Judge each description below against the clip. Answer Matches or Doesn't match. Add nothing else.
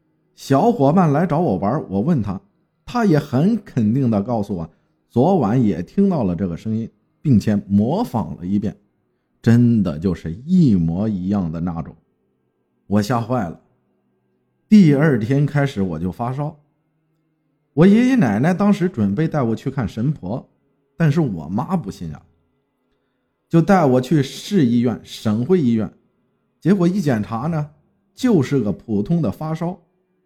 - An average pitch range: Doesn't match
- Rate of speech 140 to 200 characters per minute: Doesn't match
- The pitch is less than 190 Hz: Matches